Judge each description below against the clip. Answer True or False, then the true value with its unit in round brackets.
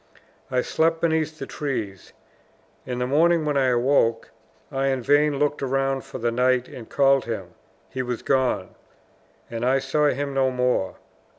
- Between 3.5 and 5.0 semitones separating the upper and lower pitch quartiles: False (2.5 semitones)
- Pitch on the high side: False (135 Hz)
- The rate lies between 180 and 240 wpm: False (165 wpm)